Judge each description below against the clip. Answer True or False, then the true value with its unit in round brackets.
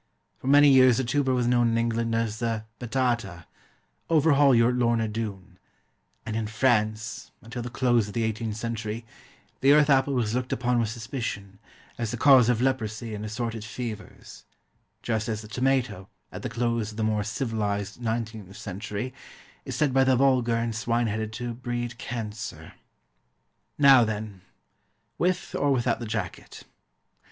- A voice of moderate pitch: False (115 Hz)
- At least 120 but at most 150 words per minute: False (160 wpm)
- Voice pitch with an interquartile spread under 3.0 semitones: True (2.4 semitones)